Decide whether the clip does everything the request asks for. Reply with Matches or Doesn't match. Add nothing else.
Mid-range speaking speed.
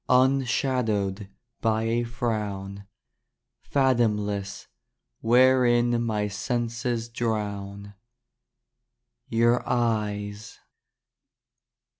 Doesn't match